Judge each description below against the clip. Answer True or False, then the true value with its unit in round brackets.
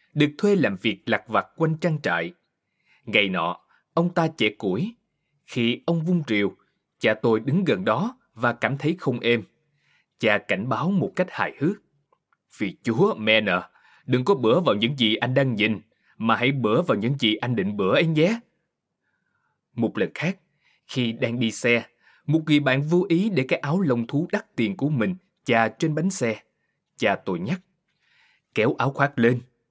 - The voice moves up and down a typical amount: False (6.7 semitones)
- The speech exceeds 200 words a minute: False (185 wpm)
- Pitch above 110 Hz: True (140 Hz)